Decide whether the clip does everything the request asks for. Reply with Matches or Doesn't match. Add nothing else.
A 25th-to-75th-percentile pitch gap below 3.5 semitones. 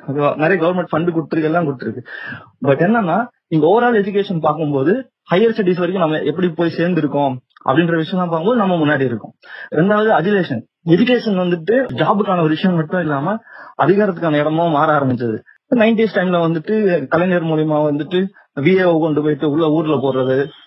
Doesn't match